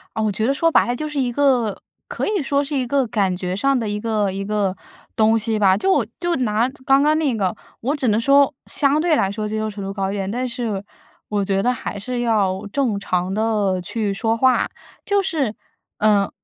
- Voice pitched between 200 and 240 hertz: Yes, high, 225 Hz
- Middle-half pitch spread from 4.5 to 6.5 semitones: Yes, average, 5.1 semitones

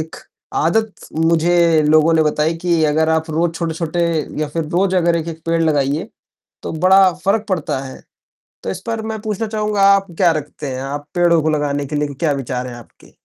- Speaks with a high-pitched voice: No, medium, 165 Hz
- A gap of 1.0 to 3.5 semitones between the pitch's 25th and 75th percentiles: Yes, average, 2.8 semitones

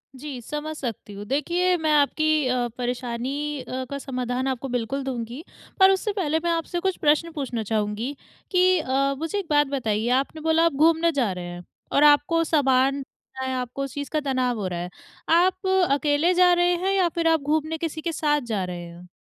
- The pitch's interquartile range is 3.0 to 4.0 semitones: No, average, 4.5 semitones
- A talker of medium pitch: No, very high, 285 Hz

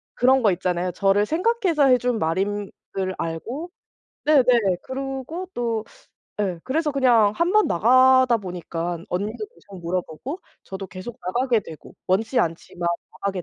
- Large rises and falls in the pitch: Yes, wide, 6.3 semitones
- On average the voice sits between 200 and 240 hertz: Yes, high, 220 Hz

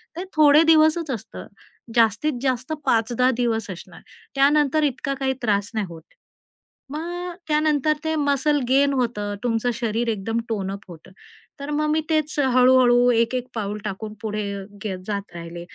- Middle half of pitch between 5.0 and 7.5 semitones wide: Yes, wide, 5.5 semitones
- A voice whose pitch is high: Yes, very high, 250 Hz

